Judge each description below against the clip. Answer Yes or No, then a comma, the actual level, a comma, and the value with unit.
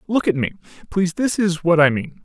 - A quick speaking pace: Yes, fast, 215 wpm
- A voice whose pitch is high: No, medium, 175 Hz